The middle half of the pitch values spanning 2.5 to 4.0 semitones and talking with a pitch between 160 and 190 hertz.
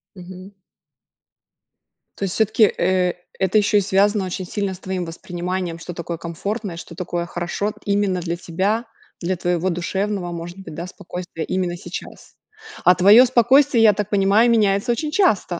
Yes: average, 2.9 semitones; medium, 185 Hz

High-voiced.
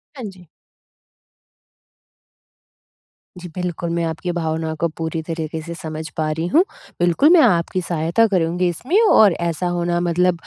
No: medium, 170 Hz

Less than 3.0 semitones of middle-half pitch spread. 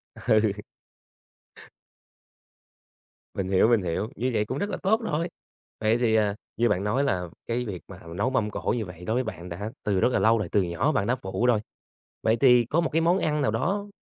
No: average, 4.5 semitones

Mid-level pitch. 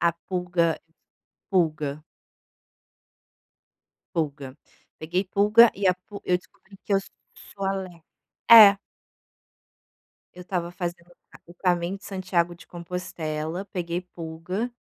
Yes: medium, 175 Hz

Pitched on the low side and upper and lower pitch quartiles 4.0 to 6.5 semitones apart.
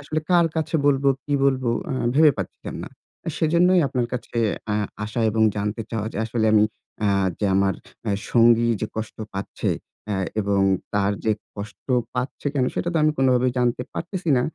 Yes: low, 120 Hz; average, 5.0 semitones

